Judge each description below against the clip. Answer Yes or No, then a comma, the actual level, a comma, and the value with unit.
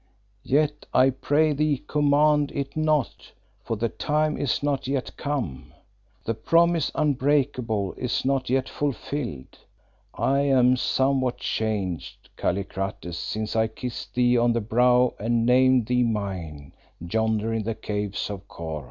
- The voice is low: Yes, low, 125 Hz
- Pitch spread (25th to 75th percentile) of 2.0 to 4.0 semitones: No, average, 4.6 semitones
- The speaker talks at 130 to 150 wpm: Yes, slow, 135 wpm